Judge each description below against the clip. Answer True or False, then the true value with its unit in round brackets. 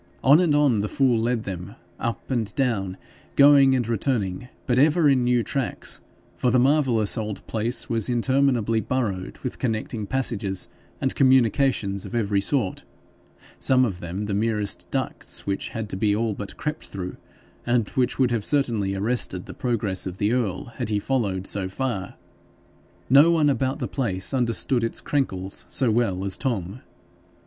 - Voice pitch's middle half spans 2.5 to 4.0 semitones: False (4.7 semitones)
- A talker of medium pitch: False (115 Hz)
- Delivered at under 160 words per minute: False (165 wpm)